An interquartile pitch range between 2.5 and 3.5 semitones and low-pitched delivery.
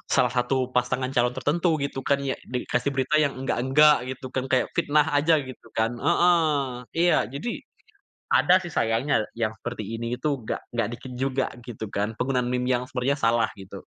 Yes: average, 2.9 semitones; low, 130 Hz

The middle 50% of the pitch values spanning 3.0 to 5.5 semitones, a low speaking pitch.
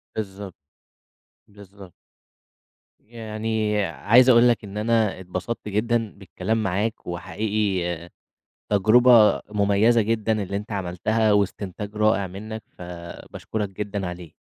No: narrow, 2.4 semitones; low, 105 Hz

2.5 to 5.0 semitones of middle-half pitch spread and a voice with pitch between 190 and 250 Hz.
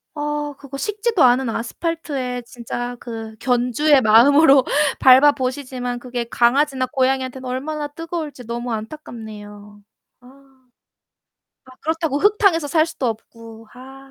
No: average, 3.5 semitones; very high, 260 Hz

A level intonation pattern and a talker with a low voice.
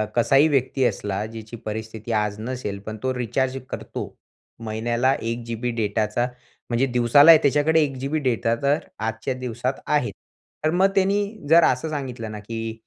No: average, 3.7 semitones; low, 120 Hz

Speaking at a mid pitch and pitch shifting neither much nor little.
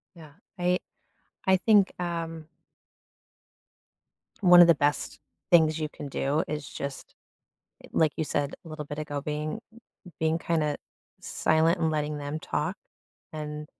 No: medium, 155 Hz; narrow, 2.0 semitones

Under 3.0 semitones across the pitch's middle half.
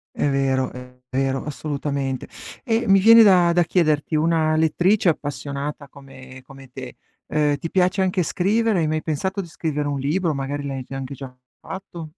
No: average, 4.5 semitones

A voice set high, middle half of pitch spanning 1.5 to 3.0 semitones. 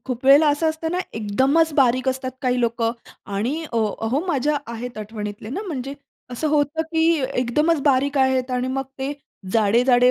No: very high, 260 Hz; average, 3.8 semitones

